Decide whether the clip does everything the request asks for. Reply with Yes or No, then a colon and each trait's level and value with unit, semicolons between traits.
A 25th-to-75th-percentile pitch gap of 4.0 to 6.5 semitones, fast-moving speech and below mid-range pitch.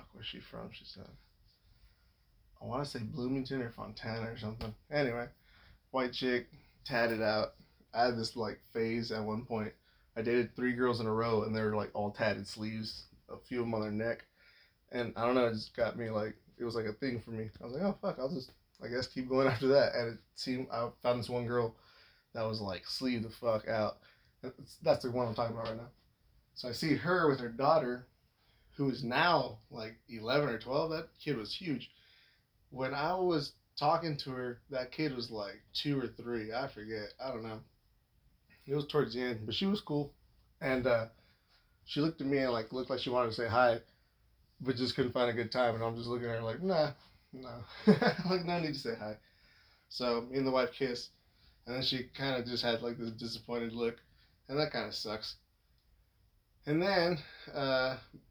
No: average, 3.1 semitones; fast, 215 wpm; low, 120 Hz